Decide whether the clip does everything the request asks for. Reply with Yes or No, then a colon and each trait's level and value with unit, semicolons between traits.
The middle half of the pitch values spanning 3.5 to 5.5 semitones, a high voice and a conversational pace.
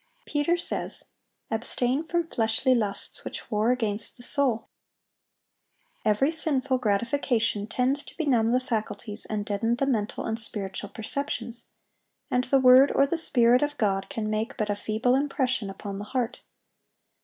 Yes: average, 4.1 semitones; high, 240 Hz; average, 150 wpm